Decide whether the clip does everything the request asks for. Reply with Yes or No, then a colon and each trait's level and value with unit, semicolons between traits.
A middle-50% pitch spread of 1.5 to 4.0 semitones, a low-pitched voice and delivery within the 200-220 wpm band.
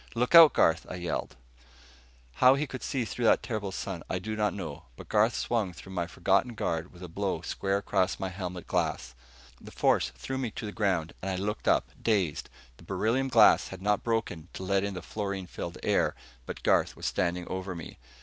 Yes: average, 3.5 semitones; very low, 95 Hz; fast, 205 wpm